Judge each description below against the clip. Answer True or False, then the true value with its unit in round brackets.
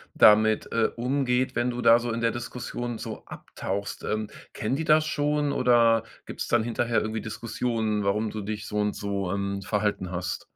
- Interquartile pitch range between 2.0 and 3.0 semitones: True (2.5 semitones)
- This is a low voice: True (115 Hz)